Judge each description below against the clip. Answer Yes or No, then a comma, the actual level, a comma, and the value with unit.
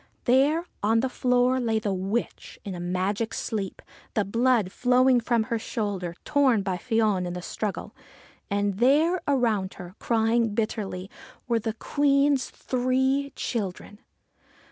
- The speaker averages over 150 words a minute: No, average, 140 wpm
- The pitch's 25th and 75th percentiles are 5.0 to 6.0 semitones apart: No, average, 4.2 semitones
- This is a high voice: Yes, high, 225 Hz